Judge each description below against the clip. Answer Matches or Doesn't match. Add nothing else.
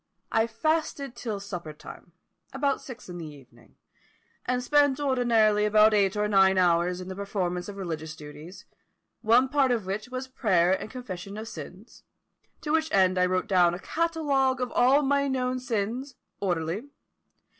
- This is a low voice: Doesn't match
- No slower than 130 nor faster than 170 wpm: Matches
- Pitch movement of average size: Doesn't match